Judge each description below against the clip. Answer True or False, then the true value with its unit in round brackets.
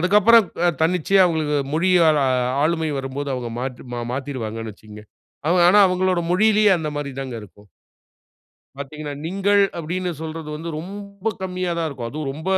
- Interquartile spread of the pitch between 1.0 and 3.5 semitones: False (4.8 semitones)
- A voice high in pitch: False (160 Hz)